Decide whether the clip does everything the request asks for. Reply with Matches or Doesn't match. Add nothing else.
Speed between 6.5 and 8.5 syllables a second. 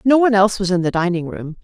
Matches